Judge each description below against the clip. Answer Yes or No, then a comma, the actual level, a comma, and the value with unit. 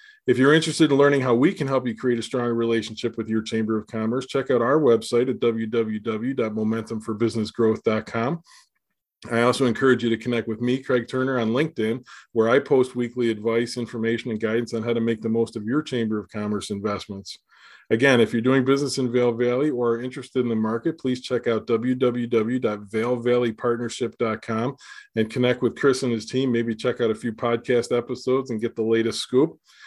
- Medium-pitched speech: No, low, 120 Hz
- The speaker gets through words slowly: No, average, 190 wpm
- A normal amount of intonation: No, narrow, 1.9 semitones